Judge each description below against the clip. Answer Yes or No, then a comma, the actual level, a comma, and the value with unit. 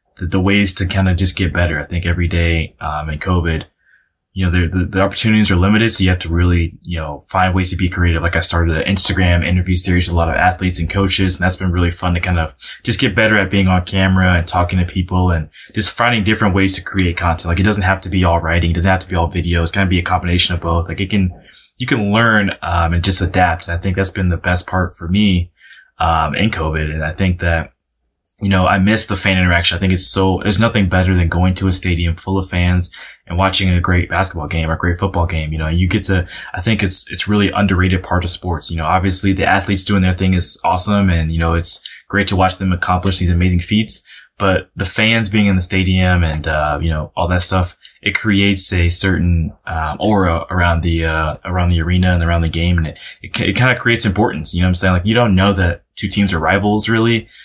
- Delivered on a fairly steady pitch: Yes, narrow, 2.2 semitones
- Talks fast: Yes, fast, 260 wpm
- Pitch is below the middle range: Yes, very low, 90 Hz